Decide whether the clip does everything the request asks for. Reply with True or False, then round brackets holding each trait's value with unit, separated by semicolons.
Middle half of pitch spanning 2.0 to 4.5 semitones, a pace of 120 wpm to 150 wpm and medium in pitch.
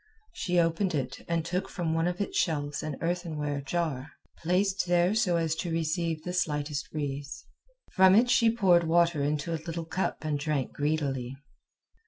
False (3.2 semitones; 170 wpm; 165 Hz)